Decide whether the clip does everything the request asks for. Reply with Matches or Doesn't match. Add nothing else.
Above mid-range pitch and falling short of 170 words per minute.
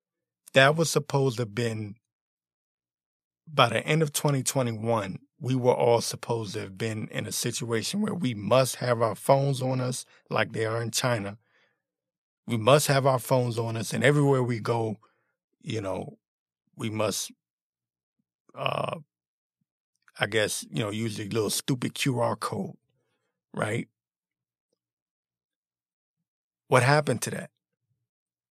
Doesn't match